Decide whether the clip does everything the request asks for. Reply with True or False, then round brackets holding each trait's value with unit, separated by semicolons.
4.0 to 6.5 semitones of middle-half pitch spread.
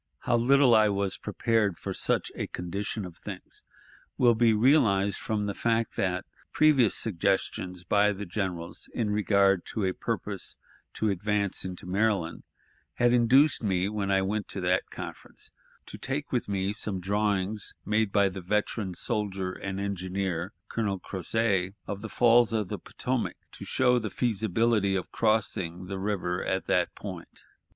False (2.9 semitones)